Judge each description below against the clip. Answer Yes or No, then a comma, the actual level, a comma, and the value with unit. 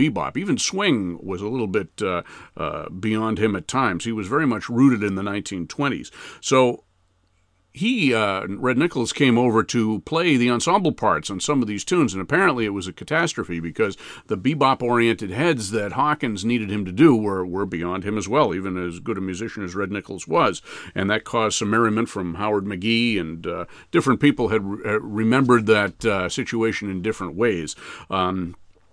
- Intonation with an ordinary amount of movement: Yes, average, 3.9 semitones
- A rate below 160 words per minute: No, average, 190 wpm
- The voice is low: Yes, low, 105 Hz